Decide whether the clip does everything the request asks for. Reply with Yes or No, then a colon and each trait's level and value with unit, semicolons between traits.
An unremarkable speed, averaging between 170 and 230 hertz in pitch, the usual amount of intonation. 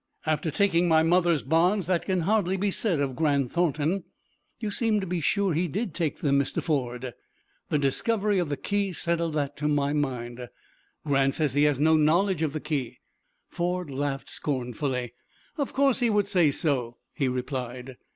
No: average, 180 wpm; medium, 155 Hz; average, 4.7 semitones